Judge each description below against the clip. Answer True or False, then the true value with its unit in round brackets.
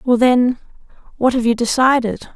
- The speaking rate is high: False (155 wpm)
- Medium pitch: False (240 Hz)